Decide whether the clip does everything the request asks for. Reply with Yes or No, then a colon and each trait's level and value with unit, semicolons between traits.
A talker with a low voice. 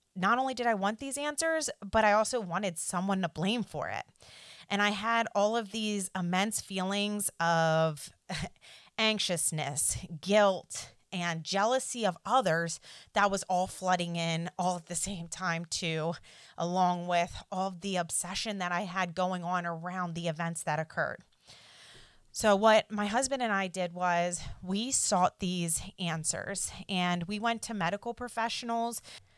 No: medium, 185 Hz